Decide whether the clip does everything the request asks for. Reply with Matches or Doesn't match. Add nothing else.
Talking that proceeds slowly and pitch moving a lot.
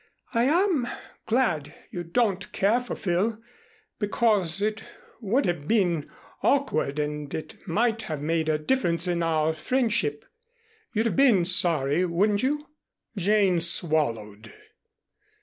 Matches